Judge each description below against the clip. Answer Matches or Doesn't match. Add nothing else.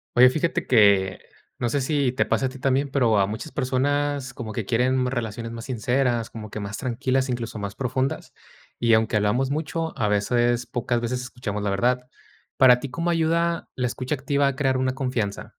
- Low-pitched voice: Matches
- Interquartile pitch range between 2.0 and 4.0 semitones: Matches